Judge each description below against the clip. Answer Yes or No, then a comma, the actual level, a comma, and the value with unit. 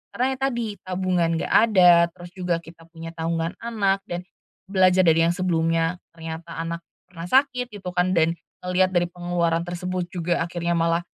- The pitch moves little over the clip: Yes, narrow, 1.9 semitones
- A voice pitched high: No, medium, 175 Hz